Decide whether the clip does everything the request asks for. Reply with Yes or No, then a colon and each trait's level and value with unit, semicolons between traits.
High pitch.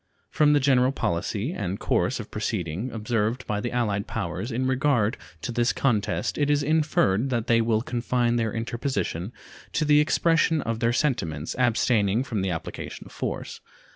No: low, 120 Hz